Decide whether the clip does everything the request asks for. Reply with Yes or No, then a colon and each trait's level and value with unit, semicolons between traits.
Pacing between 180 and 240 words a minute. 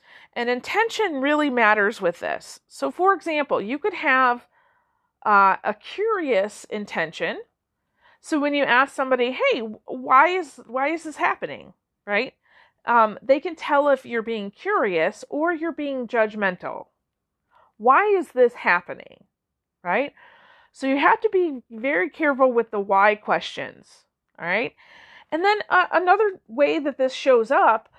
No: average, 145 wpm